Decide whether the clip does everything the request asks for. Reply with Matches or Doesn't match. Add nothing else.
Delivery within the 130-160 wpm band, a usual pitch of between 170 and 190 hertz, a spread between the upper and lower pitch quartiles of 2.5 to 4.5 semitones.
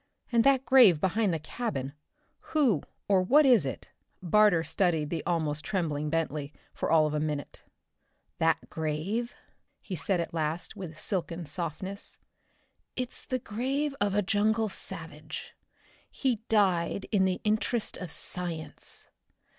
Doesn't match